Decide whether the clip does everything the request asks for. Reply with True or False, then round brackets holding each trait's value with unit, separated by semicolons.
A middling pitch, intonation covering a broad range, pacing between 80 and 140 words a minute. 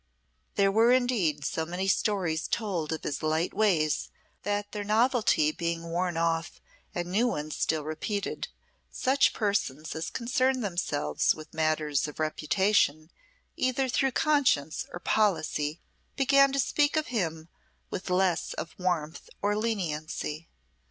True (180 Hz; 5.8 semitones; 135 wpm)